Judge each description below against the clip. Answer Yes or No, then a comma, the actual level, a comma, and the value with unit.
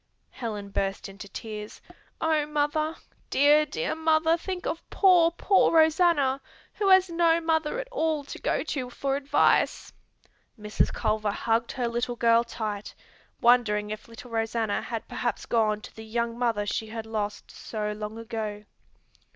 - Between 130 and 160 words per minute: Yes, average, 150 wpm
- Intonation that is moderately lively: No, wide, 6.5 semitones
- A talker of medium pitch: No, high, 235 Hz